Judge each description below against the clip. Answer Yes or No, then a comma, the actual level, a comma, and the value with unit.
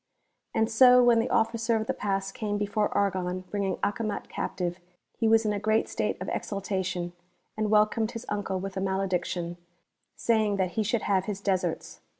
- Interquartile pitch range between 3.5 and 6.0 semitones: No, narrow, 2.6 semitones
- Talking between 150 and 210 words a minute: Yes, average, 180 wpm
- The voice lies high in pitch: Yes, high, 205 Hz